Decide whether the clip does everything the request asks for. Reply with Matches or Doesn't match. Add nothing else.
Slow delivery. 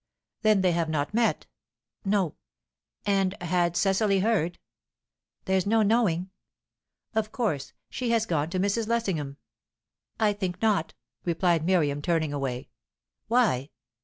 Matches